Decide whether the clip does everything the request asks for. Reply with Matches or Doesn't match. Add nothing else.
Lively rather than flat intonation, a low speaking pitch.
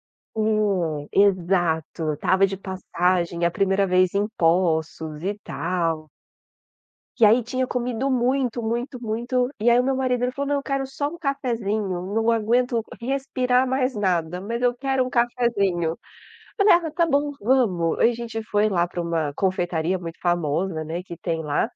Doesn't match